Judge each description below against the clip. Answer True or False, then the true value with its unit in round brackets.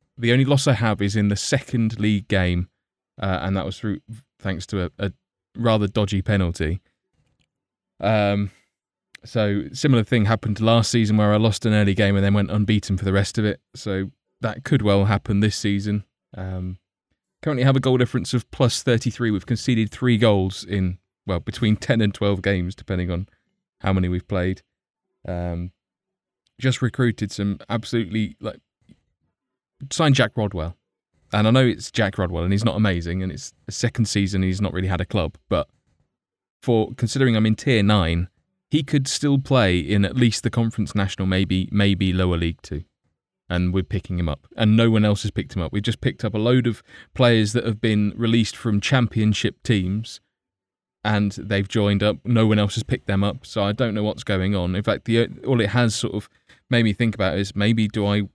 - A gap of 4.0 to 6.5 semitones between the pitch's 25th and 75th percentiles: False (3.3 semitones)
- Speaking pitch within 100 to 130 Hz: True (105 Hz)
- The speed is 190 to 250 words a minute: True (200 wpm)